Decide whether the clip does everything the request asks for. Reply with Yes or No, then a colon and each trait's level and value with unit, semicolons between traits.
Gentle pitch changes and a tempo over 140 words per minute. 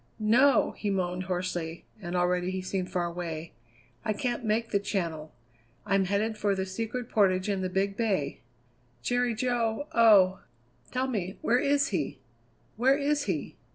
No: average, 4.1 semitones; average, 155 wpm